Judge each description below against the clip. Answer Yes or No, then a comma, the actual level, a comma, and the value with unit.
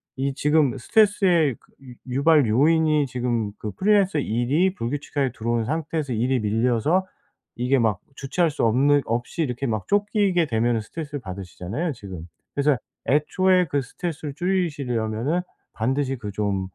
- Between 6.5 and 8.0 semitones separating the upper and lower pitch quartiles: No, wide, 5.6 semitones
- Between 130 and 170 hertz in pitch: Yes, low, 135 Hz